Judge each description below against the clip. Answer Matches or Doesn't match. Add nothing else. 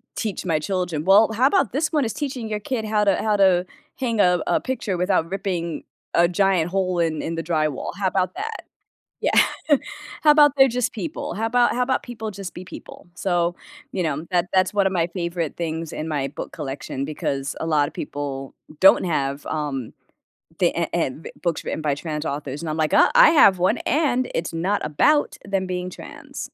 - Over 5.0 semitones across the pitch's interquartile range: Matches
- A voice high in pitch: Doesn't match